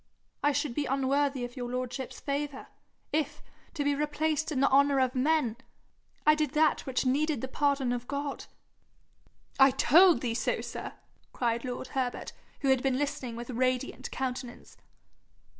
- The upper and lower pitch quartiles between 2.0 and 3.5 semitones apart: Yes, narrow, 2.4 semitones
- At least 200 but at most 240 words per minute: No, average, 160 wpm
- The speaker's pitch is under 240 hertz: No, very high, 270 Hz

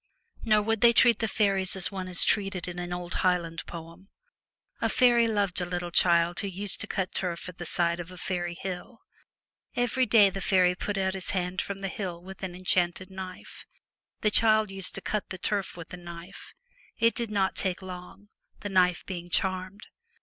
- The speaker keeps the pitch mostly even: Yes, narrow, 2.3 semitones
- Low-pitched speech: No, medium, 185 Hz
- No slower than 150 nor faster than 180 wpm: No, average, 200 wpm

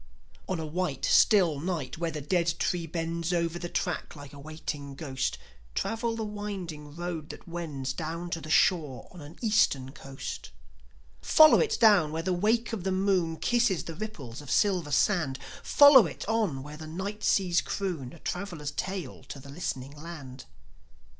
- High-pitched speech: No, medium, 170 Hz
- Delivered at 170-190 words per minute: Yes, average, 175 wpm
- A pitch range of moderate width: Yes, average, 4.5 semitones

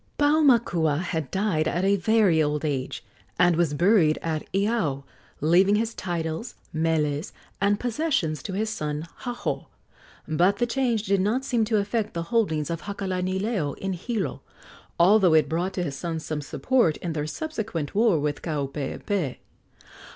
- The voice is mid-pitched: Yes, medium, 180 Hz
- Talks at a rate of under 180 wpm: Yes, average, 150 wpm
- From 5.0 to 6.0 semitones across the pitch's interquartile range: Yes, wide, 5.6 semitones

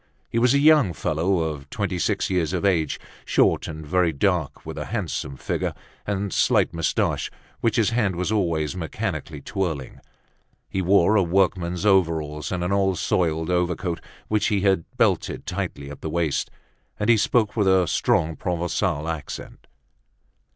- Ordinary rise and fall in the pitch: Yes, average, 3.6 semitones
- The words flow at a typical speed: Yes, average, 160 wpm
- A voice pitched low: Yes, very low, 90 Hz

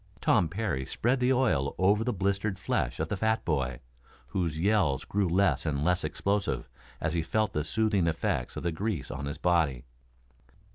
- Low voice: Yes, very low, 90 Hz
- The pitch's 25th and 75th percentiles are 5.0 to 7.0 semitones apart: Yes, wide, 5.4 semitones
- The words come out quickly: No, average, 180 wpm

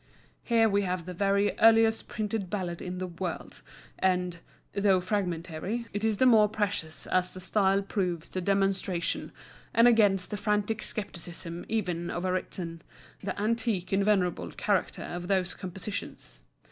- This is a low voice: No, high, 190 Hz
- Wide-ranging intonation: No, average, 2.7 semitones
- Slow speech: No, average, 150 wpm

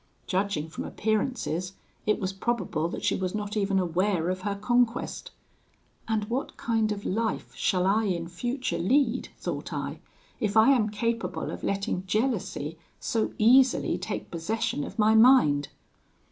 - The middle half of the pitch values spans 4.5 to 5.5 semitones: No, average, 3.9 semitones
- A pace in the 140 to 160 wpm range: Yes, average, 150 wpm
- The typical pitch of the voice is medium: No, high, 210 Hz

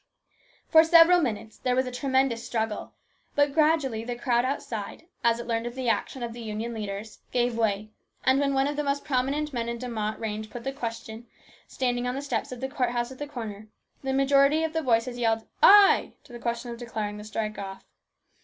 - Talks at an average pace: No, fast, 220 wpm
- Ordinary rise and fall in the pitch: Yes, average, 3.2 semitones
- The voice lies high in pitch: Yes, high, 245 Hz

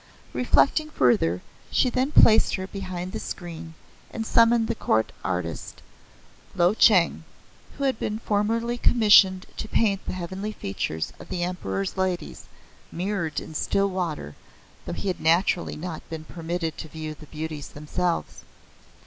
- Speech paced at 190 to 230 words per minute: No, average, 145 wpm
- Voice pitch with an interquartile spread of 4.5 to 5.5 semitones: Yes, average, 4.9 semitones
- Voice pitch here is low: No, medium, 180 Hz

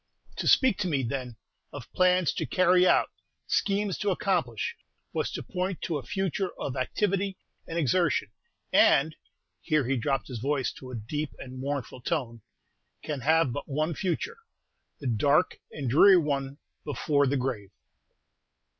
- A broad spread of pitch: Yes, wide, 5.7 semitones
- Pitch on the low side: No, medium, 145 Hz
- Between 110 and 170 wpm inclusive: Yes, average, 155 wpm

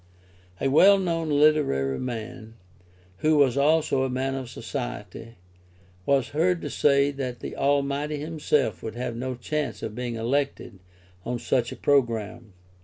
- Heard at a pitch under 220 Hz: Yes, low, 135 Hz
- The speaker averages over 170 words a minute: No, average, 145 wpm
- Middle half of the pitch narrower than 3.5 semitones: No, average, 3.8 semitones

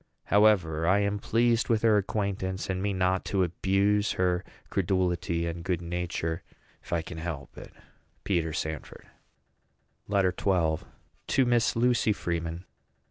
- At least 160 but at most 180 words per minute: No, slow, 135 wpm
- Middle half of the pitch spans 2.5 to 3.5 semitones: Yes, average, 3.2 semitones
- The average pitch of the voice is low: Yes, very low, 95 Hz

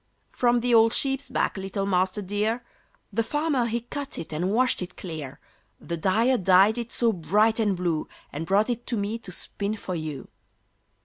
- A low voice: No, high, 210 Hz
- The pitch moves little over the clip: No, average, 4.4 semitones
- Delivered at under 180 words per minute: No, average, 185 wpm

